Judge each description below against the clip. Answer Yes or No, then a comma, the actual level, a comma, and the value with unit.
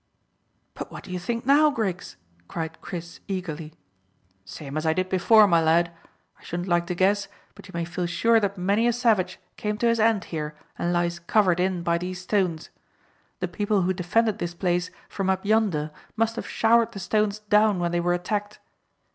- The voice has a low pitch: No, medium, 185 Hz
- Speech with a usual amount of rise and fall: Yes, average, 3.5 semitones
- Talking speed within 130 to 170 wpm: No, average, 195 wpm